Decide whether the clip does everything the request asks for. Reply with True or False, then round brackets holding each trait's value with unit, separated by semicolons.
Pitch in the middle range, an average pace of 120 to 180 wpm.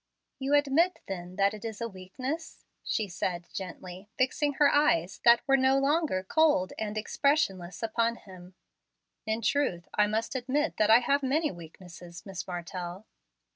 False (220 Hz; 155 wpm)